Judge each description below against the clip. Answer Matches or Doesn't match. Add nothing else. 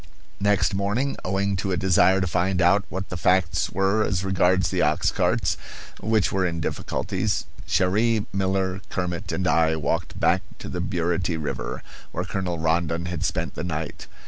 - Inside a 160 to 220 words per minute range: Matches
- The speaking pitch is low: Matches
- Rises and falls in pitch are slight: Matches